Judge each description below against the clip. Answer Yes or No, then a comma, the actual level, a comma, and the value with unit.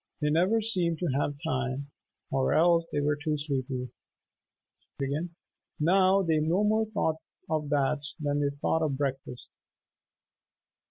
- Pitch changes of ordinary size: Yes, average, 3.1 semitones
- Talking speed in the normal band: No, slow, 130 wpm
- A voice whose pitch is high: No, medium, 150 Hz